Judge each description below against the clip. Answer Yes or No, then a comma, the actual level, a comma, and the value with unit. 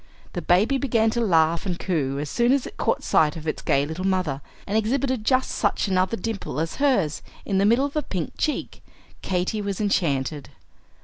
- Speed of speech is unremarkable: Yes, average, 195 wpm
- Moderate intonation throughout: No, wide, 6.2 semitones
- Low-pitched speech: No, high, 195 Hz